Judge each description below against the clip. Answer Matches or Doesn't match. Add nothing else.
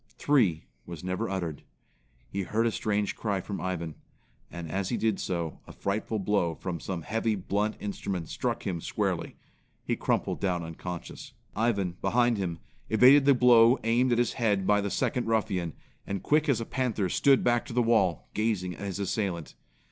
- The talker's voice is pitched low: Matches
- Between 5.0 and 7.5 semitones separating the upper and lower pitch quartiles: Doesn't match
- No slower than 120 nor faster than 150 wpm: Doesn't match